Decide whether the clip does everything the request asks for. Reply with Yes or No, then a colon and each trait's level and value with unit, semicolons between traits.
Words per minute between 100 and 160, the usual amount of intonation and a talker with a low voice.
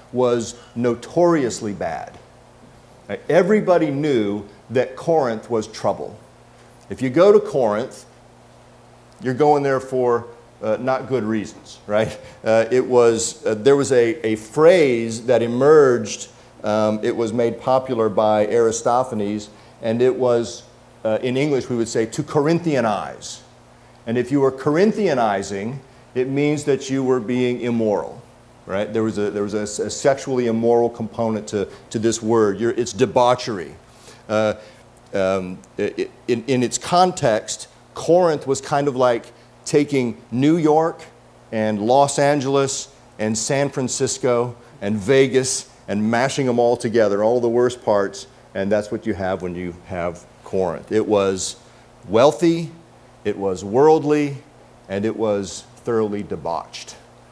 Yes: average, 140 wpm; average, 3.8 semitones; low, 120 Hz